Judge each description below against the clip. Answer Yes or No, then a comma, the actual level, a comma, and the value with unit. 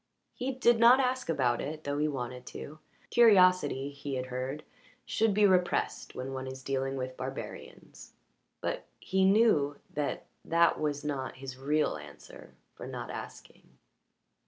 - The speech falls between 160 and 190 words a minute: No, average, 150 wpm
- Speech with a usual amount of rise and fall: No, wide, 6.1 semitones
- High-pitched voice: No, medium, 145 Hz